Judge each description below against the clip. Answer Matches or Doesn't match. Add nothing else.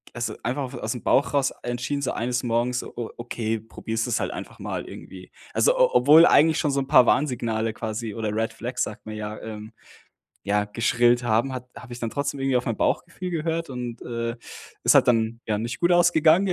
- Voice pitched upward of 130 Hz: Doesn't match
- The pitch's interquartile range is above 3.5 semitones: Matches